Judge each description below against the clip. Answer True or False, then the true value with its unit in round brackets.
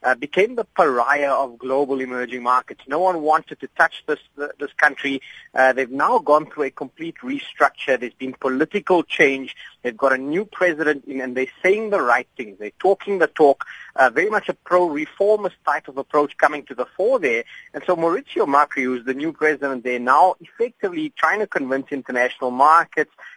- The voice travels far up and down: True (5.9 semitones)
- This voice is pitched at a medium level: True (150 Hz)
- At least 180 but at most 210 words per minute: True (195 wpm)